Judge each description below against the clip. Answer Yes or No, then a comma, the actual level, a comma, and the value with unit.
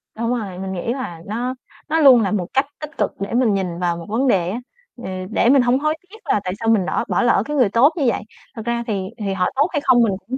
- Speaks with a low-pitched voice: No, high, 230 Hz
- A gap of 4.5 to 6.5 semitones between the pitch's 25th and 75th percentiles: Yes, average, 5.1 semitones